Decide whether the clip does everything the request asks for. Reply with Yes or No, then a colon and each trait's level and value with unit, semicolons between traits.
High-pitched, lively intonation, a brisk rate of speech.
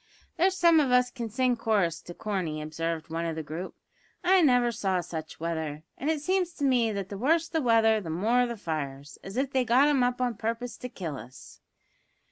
Yes: high, 225 Hz; wide, 7.4 semitones; fast, 215 wpm